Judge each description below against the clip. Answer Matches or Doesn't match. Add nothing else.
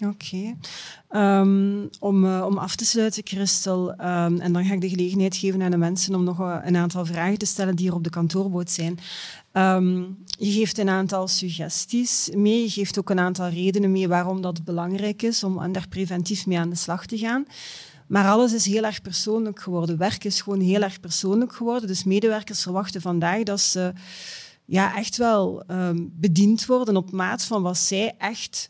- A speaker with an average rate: Matches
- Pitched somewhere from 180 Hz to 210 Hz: Matches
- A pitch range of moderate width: Doesn't match